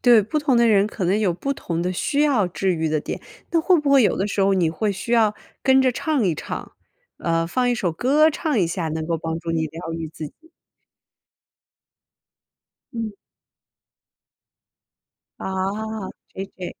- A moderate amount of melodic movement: No, wide, 7.3 semitones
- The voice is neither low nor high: No, high, 200 Hz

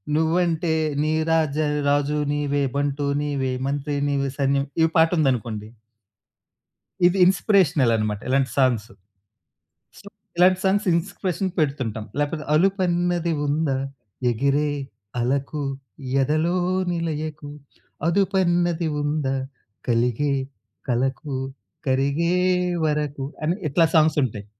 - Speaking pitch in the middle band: Yes, medium, 150 Hz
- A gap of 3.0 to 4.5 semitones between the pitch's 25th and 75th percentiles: Yes, average, 3.8 semitones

